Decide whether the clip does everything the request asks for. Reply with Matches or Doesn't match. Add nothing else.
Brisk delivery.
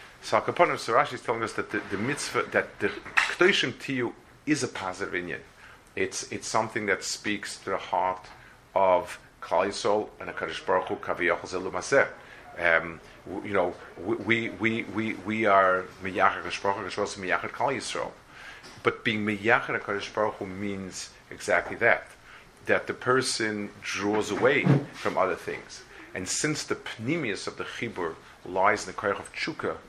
Doesn't match